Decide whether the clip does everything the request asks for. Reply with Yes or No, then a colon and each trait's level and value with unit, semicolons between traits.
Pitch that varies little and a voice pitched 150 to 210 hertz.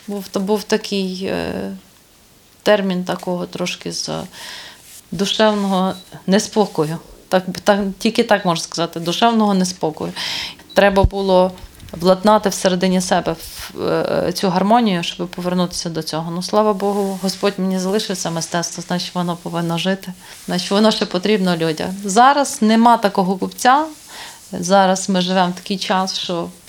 Yes: narrow, 2.3 semitones; high, 190 Hz